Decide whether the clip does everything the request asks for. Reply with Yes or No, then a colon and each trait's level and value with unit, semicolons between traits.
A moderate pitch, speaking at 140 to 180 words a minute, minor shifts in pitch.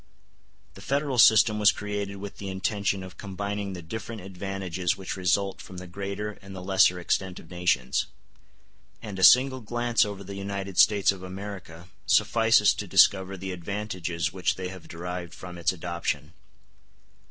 No: very low, 95 Hz; average, 160 wpm; narrow, 2.2 semitones